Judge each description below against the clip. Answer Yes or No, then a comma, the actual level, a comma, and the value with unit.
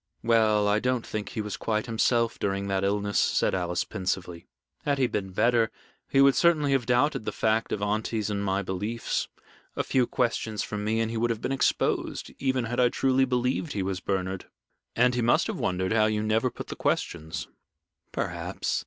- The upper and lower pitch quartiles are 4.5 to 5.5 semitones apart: No, average, 3.6 semitones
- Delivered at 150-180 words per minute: No, average, 195 wpm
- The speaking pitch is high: No, low, 110 Hz